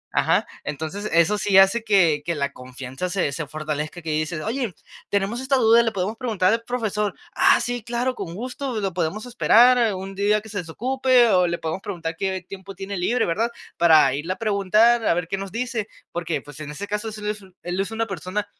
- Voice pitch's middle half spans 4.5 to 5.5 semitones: Yes, average, 4.8 semitones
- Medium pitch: No, high, 195 Hz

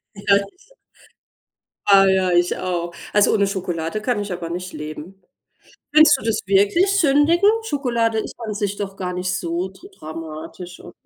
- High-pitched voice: Yes, high, 195 Hz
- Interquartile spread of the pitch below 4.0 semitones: No, average, 4.5 semitones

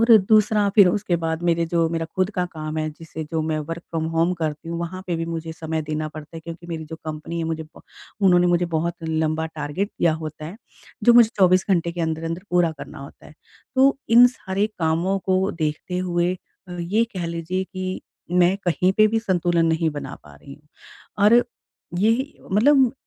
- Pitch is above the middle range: No, medium, 170 Hz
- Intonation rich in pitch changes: No, average, 2.8 semitones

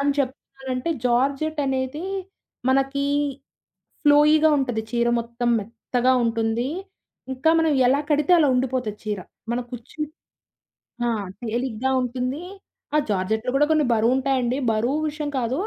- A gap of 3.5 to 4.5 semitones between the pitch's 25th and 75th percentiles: No, average, 3.0 semitones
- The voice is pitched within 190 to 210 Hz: No, very high, 255 Hz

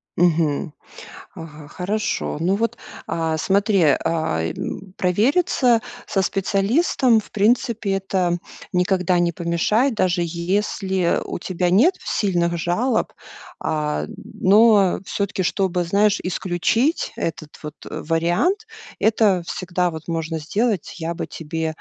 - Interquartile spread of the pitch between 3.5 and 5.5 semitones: Yes, average, 3.8 semitones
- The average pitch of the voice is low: No, medium, 185 Hz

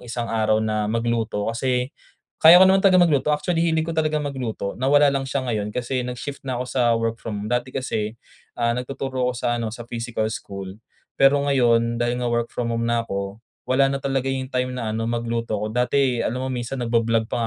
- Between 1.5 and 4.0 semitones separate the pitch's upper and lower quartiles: Yes, average, 2.7 semitones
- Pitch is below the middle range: Yes, low, 120 Hz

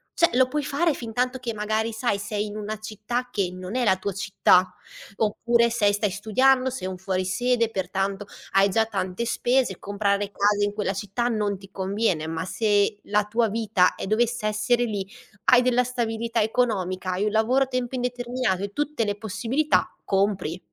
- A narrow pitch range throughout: No, average, 3.5 semitones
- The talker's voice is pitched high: Yes, high, 215 Hz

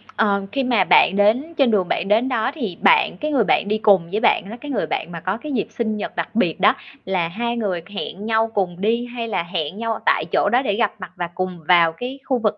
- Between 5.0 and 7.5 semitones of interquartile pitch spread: No, average, 4.2 semitones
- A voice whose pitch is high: Yes, high, 210 Hz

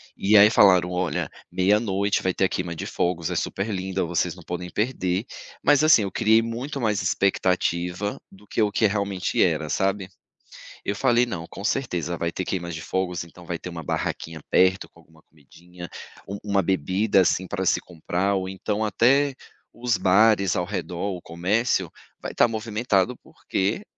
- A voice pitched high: No, very low, 95 Hz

